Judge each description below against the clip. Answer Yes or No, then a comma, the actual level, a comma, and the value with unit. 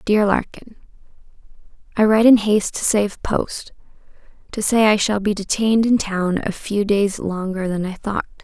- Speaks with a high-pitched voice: Yes, high, 205 Hz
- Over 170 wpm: No, average, 165 wpm